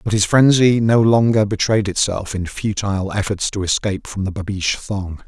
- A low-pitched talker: Yes, low, 100 Hz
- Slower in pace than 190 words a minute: Yes, average, 180 wpm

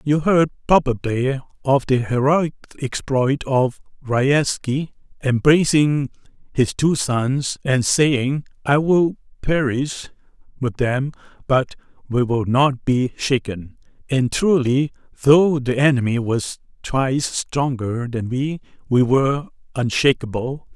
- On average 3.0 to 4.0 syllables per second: Yes, 3.7 syllables/s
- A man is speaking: Yes, male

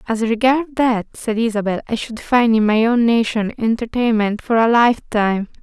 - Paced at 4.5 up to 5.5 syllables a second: Yes, 5.0 syllables/s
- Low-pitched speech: No, high, 225 Hz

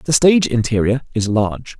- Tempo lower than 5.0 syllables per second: No, 5.7 syllables/s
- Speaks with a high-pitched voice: No, low, 120 Hz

